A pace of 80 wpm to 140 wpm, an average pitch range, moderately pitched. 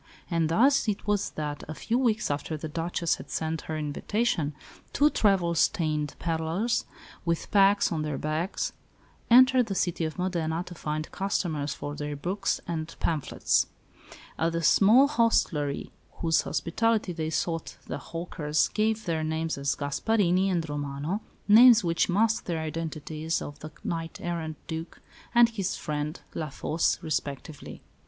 No: average, 150 wpm; average, 4.3 semitones; medium, 165 Hz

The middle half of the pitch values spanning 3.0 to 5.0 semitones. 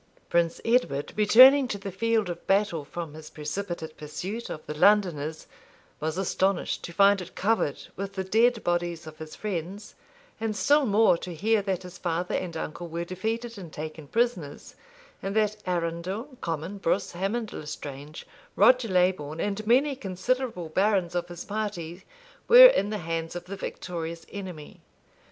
Yes: average, 4.2 semitones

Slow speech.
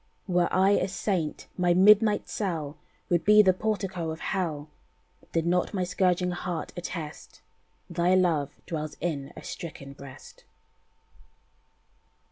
Yes: slow, 125 wpm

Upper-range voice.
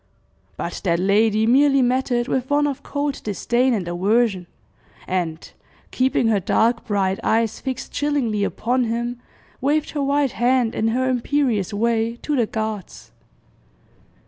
Yes: high, 235 Hz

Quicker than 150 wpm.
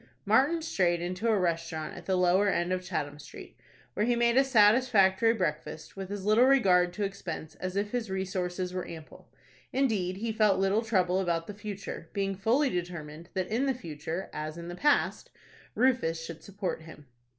Yes: average, 185 wpm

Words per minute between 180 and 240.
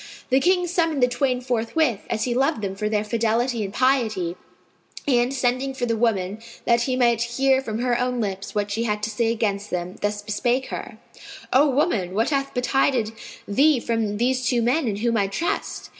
Yes: average, 195 wpm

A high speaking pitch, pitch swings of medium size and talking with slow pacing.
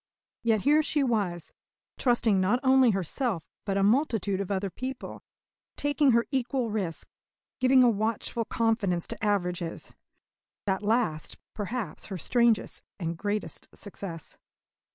Yes: high, 215 Hz; average, 4.3 semitones; slow, 130 wpm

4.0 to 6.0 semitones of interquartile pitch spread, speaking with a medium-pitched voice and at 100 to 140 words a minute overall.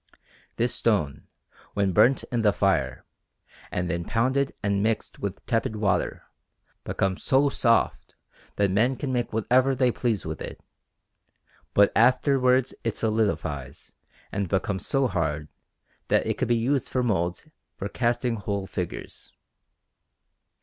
No: average, 4.3 semitones; low, 110 Hz; slow, 135 wpm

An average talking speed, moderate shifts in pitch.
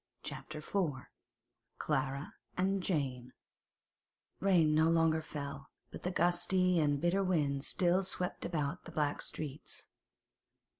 No: slow, 115 wpm; average, 3.9 semitones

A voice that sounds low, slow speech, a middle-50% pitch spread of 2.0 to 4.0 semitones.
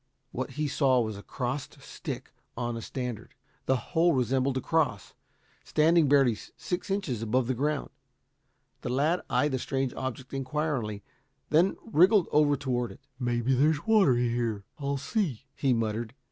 No: low, 130 Hz; average, 155 wpm; average, 3.7 semitones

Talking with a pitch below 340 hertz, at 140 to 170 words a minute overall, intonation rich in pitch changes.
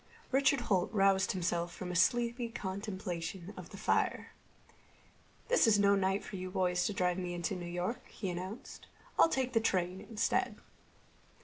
No: high, 190 Hz; average, 165 wpm; average, 3.8 semitones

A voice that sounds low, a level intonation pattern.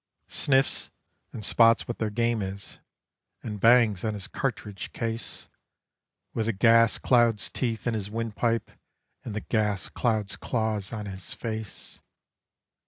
Yes: low, 110 Hz; narrow, 1.8 semitones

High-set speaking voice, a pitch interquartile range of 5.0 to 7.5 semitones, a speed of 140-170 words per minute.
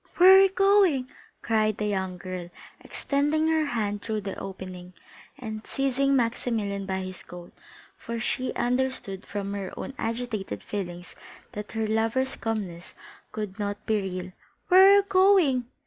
Yes: high, 220 Hz; wide, 5.6 semitones; average, 150 wpm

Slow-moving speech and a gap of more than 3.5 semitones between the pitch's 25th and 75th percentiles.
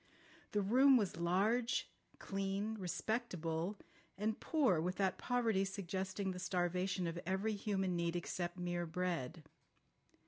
No: slow, 125 wpm; average, 3.0 semitones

